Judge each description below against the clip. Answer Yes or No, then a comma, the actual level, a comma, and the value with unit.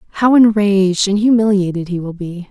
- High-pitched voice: Yes, high, 200 Hz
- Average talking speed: Yes, average, 170 wpm